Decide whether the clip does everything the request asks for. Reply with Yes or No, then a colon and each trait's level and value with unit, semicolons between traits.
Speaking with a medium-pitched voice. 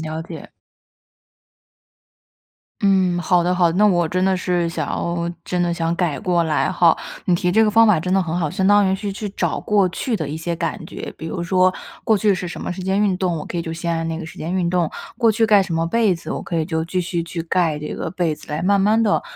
Yes: medium, 175 Hz